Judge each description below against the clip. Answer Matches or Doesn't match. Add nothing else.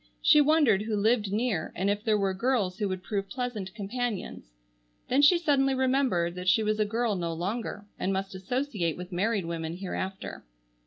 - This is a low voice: Doesn't match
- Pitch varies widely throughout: Doesn't match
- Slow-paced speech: Doesn't match